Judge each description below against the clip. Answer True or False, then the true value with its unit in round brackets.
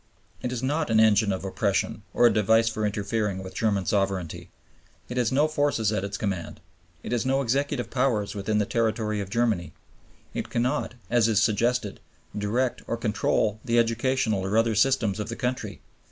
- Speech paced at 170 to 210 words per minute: True (180 wpm)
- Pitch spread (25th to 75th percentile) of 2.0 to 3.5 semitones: True (3.0 semitones)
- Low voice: True (110 Hz)